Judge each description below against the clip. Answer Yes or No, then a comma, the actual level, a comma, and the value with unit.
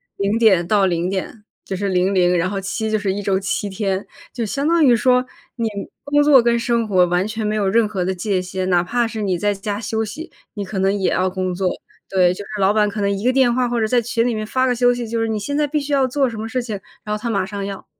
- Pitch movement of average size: Yes, average, 3.7 semitones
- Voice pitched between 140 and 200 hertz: No, high, 210 Hz